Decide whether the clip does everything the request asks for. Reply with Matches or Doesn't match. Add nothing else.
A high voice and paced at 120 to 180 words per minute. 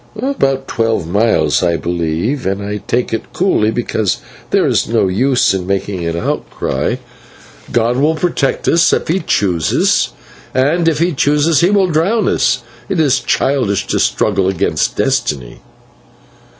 Doesn't match